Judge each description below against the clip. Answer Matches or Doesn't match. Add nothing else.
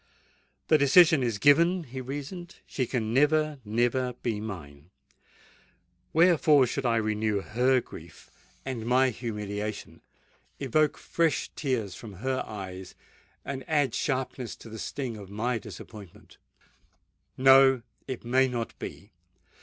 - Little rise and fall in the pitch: Doesn't match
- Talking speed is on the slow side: Matches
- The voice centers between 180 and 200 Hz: Doesn't match